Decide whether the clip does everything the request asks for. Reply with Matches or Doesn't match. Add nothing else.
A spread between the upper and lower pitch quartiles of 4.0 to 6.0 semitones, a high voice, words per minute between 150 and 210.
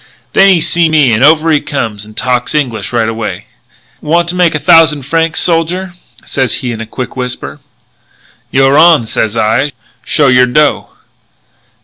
Doesn't match